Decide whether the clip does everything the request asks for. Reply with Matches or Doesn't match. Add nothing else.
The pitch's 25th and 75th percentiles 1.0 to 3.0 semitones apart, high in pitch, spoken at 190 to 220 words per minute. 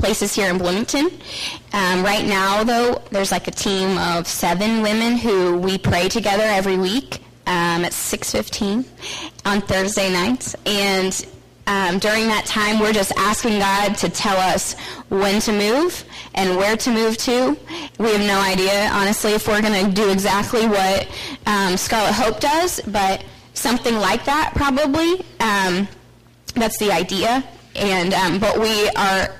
Doesn't match